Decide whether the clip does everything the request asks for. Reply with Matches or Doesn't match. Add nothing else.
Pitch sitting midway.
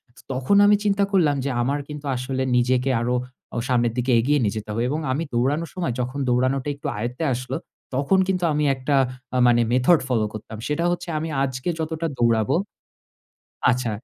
Doesn't match